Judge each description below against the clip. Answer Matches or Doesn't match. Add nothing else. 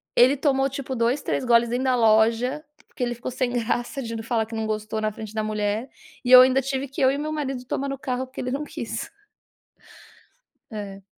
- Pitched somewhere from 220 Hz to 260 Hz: Matches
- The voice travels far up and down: Doesn't match